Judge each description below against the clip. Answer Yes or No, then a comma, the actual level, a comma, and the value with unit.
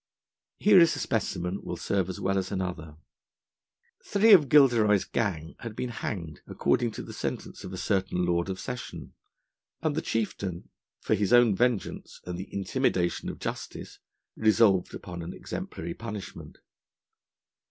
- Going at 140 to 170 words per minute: Yes, average, 150 wpm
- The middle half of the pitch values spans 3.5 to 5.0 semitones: Yes, average, 4.6 semitones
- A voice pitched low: Yes, low, 100 Hz